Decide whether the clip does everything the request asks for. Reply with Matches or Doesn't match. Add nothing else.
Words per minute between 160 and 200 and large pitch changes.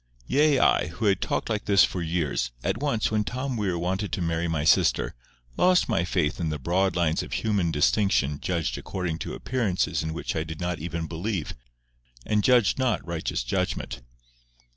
Doesn't match